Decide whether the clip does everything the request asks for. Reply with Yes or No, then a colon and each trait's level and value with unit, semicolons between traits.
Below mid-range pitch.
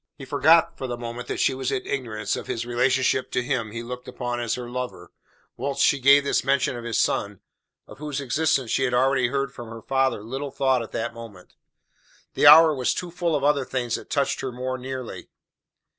Yes: low, 130 Hz